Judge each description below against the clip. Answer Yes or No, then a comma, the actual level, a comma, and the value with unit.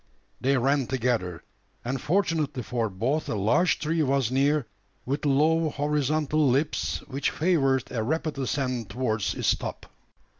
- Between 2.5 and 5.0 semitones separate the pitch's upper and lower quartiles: Yes, average, 3.4 semitones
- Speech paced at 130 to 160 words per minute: Yes, average, 140 wpm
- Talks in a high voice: No, low, 135 Hz